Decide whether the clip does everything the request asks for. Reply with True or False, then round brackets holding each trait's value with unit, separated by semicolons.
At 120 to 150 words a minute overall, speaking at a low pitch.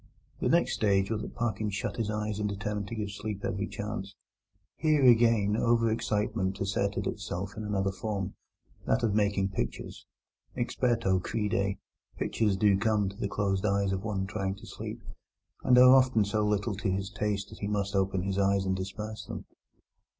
False (175 wpm; 105 Hz)